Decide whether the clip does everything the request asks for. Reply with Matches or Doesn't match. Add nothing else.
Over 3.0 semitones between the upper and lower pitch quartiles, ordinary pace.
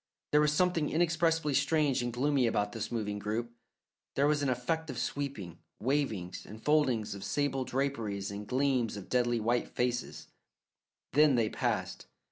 Matches